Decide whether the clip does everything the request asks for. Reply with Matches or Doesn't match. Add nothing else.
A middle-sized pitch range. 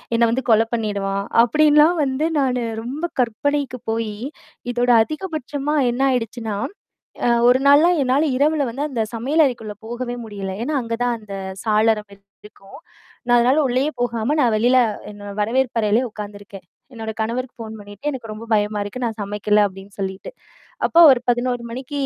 Matches